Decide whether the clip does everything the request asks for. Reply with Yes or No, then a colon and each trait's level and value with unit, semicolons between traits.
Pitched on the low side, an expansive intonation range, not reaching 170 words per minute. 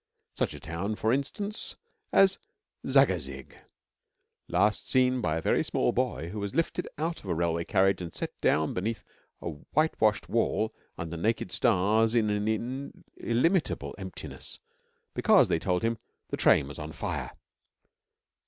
Yes: low, 105 Hz; wide, 6.1 semitones; average, 145 wpm